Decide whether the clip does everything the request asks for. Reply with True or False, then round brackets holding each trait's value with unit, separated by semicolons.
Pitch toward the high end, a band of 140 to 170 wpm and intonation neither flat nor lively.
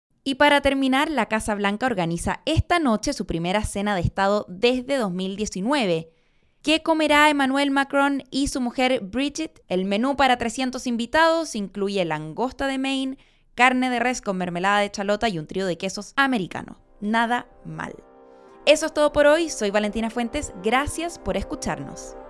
False (240 Hz; 160 wpm; 5.7 semitones)